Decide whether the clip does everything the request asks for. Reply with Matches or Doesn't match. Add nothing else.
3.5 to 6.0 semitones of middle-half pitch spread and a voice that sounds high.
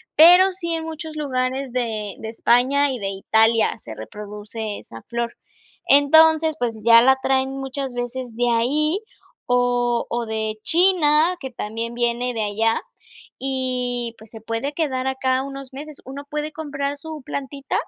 Matches